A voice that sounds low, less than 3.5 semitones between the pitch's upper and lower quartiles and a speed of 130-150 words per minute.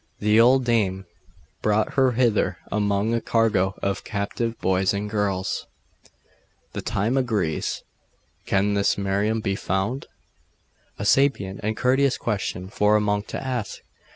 Yes: low, 105 Hz; average, 2.9 semitones; slow, 135 wpm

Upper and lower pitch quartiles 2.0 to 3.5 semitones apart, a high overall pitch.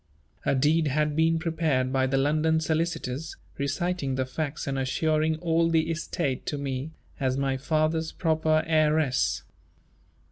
No: average, 2.9 semitones; medium, 155 Hz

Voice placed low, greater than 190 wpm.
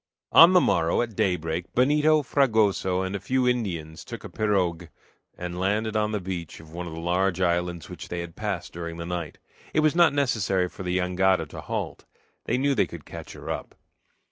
Yes: very low, 95 Hz; average, 200 wpm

